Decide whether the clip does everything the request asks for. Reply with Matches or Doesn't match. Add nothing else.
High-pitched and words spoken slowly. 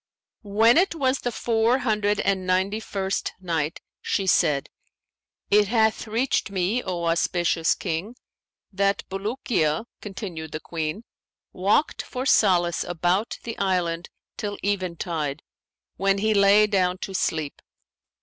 Matches